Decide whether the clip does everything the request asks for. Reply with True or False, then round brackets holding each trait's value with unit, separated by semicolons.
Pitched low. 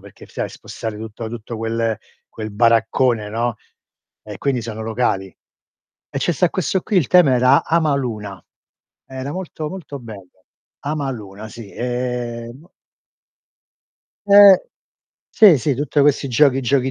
True (125 Hz)